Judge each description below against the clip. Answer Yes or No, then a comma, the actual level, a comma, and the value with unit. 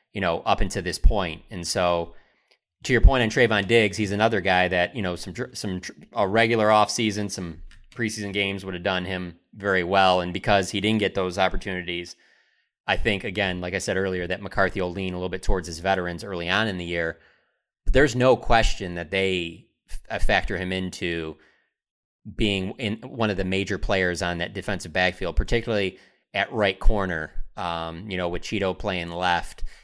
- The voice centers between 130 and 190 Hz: No, very low, 95 Hz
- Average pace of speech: Yes, average, 190 wpm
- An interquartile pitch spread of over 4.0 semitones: No, narrow, 2.6 semitones